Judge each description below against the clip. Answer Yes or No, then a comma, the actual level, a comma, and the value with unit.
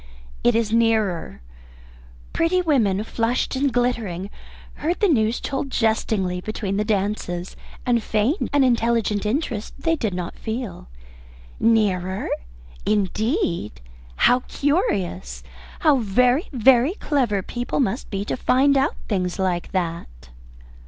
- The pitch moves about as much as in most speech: Yes, average, 5.0 semitones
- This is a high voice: Yes, high, 225 Hz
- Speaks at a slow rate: Yes, slow, 120 wpm